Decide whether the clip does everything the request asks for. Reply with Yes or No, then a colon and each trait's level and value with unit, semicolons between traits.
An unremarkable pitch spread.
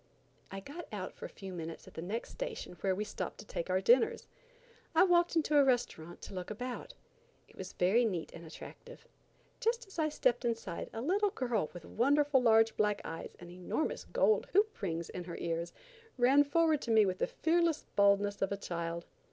No: wide, 8.5 semitones